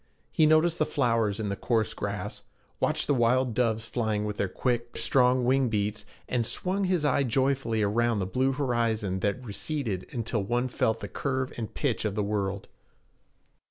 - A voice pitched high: No, low, 120 Hz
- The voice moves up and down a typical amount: Yes, average, 3.7 semitones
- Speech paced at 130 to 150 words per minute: No, average, 175 wpm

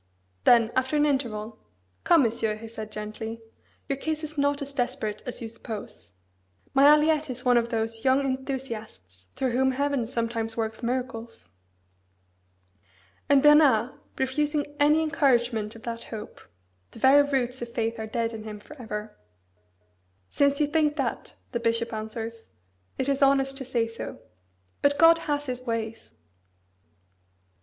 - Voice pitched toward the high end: Yes, high, 245 Hz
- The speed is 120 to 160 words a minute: Yes, average, 150 wpm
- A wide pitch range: No, average, 3.8 semitones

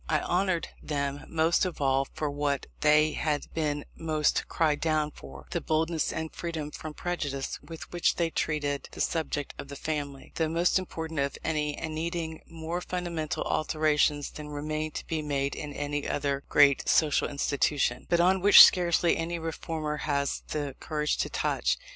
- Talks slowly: No, average, 170 wpm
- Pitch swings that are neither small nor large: No, narrow, 2.1 semitones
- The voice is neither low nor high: Yes, medium, 155 Hz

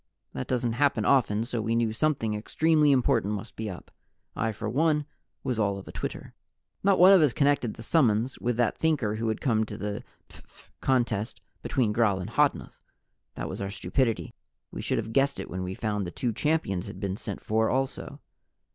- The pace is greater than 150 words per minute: Yes, average, 200 wpm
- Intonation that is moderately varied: Yes, average, 4.3 semitones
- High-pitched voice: No, low, 115 Hz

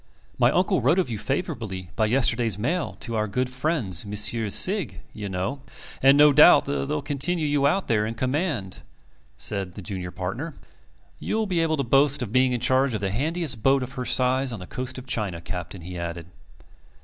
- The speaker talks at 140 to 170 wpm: No, average, 190 wpm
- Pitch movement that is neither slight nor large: No, wide, 5.8 semitones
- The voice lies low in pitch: Yes, low, 125 Hz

